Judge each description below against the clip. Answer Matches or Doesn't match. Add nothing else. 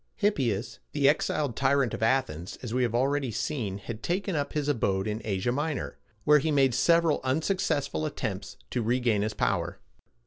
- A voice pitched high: Doesn't match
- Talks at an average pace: Matches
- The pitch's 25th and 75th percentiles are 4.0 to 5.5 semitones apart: Matches